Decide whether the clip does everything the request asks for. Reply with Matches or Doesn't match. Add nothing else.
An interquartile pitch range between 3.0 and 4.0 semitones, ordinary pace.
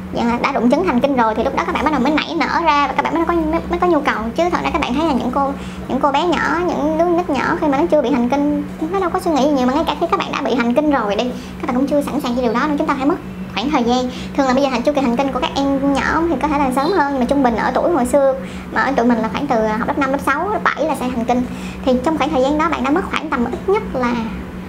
Doesn't match